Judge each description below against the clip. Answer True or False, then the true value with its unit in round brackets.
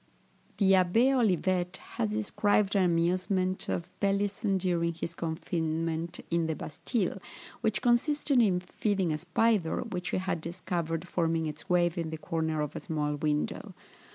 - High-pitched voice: False (180 Hz)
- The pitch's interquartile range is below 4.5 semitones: True (3.3 semitones)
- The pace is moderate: True (150 wpm)